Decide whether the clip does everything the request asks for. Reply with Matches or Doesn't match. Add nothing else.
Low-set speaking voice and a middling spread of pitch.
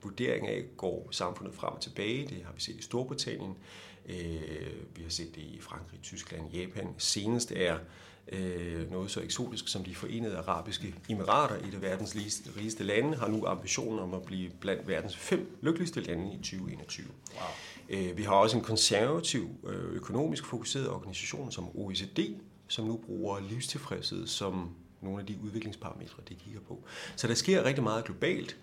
Matches